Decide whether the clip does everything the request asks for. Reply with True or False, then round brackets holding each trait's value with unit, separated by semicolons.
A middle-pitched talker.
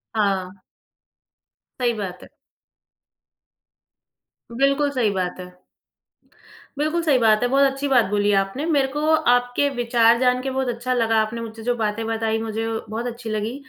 False (235 Hz)